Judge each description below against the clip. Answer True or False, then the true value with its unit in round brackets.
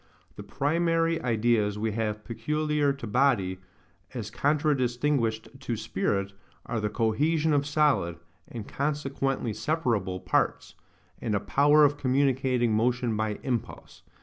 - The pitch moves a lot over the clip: False (5.0 semitones)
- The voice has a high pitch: False (125 Hz)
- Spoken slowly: True (120 wpm)